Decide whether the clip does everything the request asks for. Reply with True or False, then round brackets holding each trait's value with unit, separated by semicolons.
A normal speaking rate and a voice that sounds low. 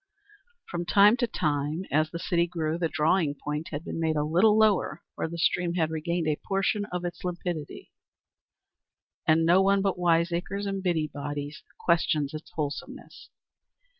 False (160 wpm; 170 Hz)